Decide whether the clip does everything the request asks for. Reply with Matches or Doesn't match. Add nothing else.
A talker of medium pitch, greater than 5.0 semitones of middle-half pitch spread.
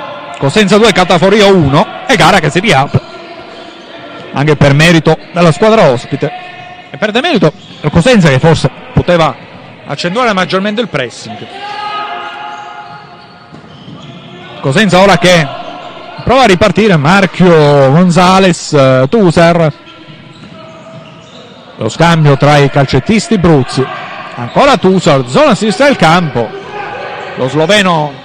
Matches